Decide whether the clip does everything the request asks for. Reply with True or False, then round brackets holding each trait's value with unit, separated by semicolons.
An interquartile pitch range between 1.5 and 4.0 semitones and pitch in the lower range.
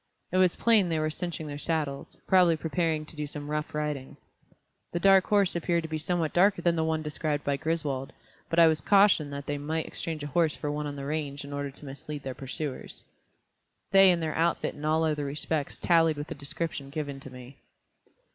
False (2.7 semitones; 155 Hz)